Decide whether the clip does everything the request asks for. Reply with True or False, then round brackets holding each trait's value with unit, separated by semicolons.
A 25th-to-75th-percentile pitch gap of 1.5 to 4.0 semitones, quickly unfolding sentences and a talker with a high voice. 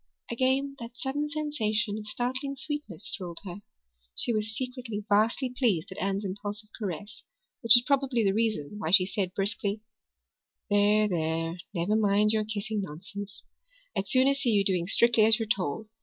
False (3.5 semitones; 160 wpm; 215 Hz)